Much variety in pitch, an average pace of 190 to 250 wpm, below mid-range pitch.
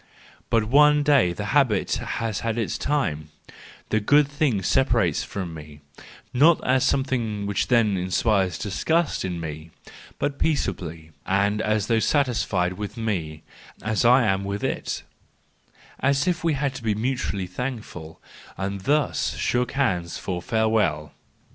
No: wide, 6.2 semitones; average, 140 wpm; low, 110 Hz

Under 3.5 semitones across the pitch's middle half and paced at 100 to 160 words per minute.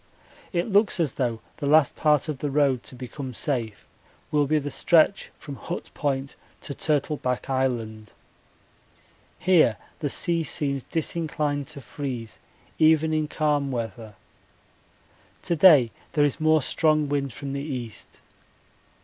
Yes: average, 3.1 semitones; average, 140 wpm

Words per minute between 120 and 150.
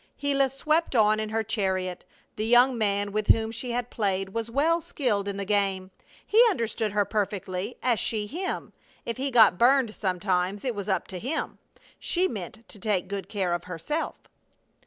No: average, 180 wpm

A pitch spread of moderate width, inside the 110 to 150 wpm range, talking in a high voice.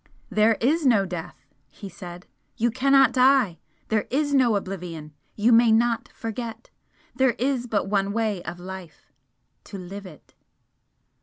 Yes: average, 4.5 semitones; average, 145 wpm; high, 220 Hz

